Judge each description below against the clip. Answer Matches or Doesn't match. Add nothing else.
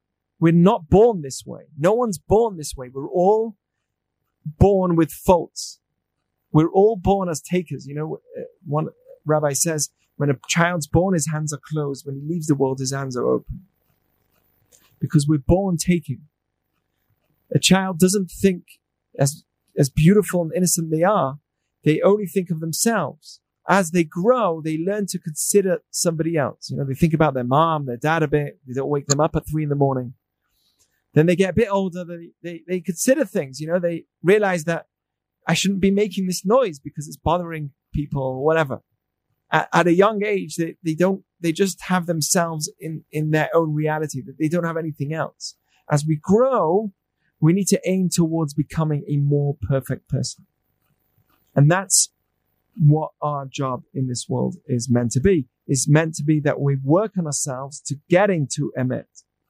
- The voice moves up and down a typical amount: Matches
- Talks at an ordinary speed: Matches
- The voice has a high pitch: Doesn't match